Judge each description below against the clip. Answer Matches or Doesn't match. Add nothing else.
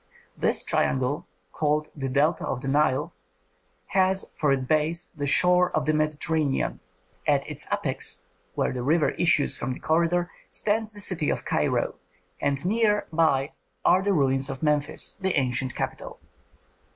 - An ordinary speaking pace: Matches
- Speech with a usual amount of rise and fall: Matches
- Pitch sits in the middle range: Matches